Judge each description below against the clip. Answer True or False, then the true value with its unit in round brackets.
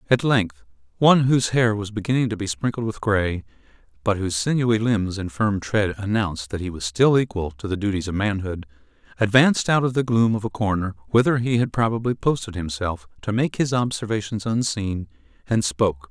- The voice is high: False (105 Hz)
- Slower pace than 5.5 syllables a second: False (5.6 syllables/s)